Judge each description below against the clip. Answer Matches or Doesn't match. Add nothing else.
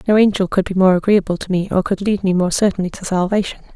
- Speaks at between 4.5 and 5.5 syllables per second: Doesn't match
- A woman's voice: Matches